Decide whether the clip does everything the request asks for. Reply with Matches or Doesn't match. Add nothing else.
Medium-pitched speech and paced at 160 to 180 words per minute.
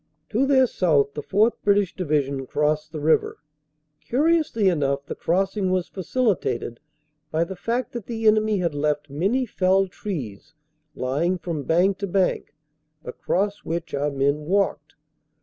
Doesn't match